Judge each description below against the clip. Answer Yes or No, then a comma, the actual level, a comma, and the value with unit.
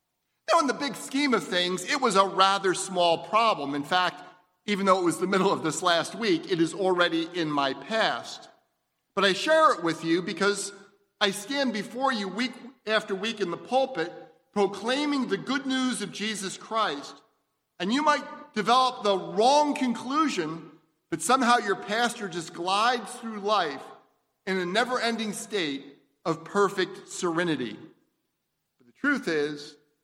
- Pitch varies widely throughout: Yes, wide, 6.1 semitones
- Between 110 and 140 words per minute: No, average, 165 wpm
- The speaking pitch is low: No, high, 200 Hz